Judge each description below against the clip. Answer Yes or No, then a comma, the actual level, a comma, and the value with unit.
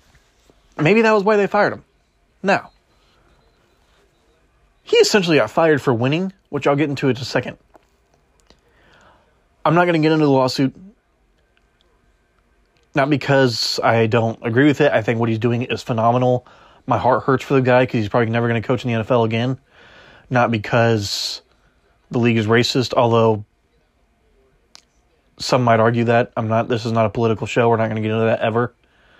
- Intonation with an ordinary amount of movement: Yes, average, 3.5 semitones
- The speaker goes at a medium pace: Yes, average, 180 wpm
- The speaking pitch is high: No, low, 120 Hz